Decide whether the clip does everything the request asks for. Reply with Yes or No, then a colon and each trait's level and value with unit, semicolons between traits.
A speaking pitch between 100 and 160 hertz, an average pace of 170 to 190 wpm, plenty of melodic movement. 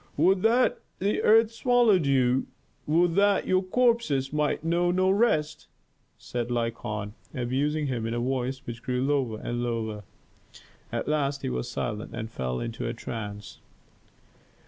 No: low, 135 Hz; average, 145 wpm; wide, 7.5 semitones